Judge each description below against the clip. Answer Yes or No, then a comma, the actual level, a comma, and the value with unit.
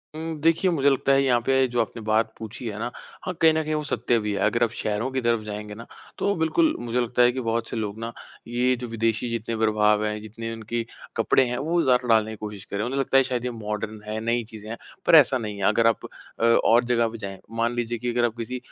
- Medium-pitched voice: No, low, 115 Hz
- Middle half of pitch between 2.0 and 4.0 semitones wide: Yes, narrow, 2.6 semitones